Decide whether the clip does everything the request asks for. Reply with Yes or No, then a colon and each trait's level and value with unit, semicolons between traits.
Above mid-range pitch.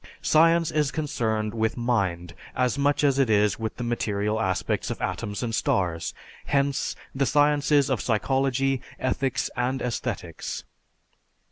No: low, 125 Hz